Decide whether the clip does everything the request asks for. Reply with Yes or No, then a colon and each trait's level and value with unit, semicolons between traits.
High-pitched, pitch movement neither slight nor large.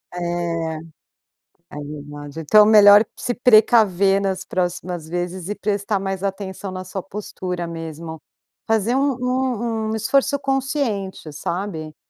Yes: high, 195 Hz; average, 4.1 semitones